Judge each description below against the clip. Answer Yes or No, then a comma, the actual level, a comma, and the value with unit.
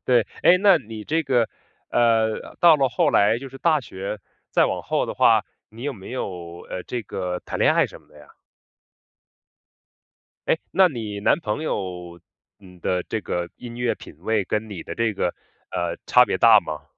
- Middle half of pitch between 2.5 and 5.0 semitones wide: No, wide, 5.5 semitones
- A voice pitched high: No, low, 110 Hz